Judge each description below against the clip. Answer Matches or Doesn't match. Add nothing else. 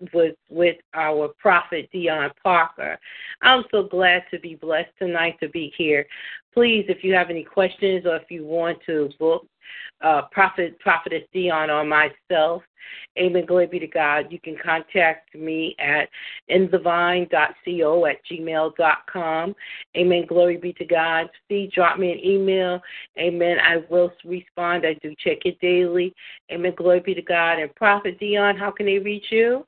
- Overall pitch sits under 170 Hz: Doesn't match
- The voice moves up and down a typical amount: Doesn't match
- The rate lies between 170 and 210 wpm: Doesn't match